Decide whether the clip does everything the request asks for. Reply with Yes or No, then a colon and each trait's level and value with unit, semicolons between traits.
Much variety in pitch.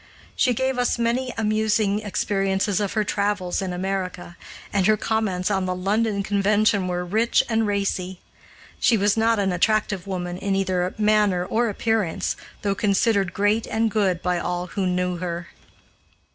No: average, 2.9 semitones